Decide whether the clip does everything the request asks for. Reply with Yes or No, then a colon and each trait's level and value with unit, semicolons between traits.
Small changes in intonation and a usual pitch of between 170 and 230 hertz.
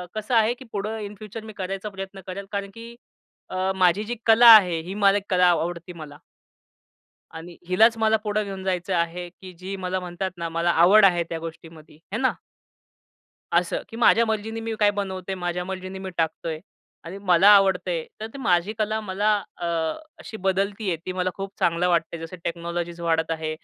No: average, 3.3 semitones; high, 190 Hz